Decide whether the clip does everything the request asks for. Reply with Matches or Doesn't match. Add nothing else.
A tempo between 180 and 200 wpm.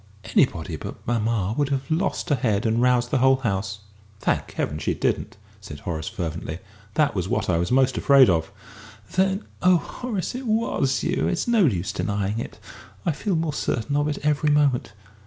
Matches